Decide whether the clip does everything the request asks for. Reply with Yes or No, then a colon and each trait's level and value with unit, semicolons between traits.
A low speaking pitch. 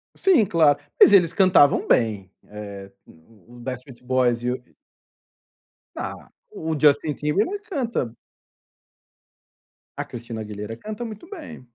Yes: low, 130 Hz